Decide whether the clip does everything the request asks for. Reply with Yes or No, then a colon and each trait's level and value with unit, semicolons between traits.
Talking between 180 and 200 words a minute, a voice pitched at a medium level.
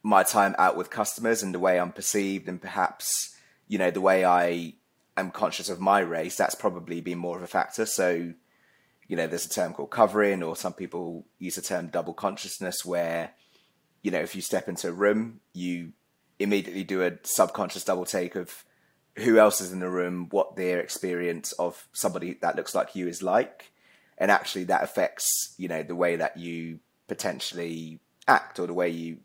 No: average, 195 wpm; very low, 90 Hz